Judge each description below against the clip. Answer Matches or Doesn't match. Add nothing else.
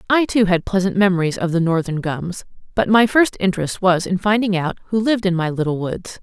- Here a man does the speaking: Doesn't match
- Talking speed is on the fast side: Matches